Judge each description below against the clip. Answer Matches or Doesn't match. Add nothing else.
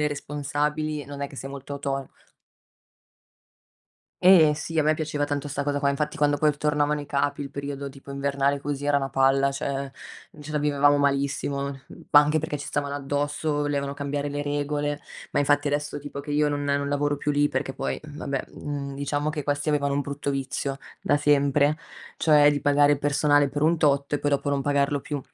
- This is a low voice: Doesn't match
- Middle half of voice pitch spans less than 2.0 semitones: Matches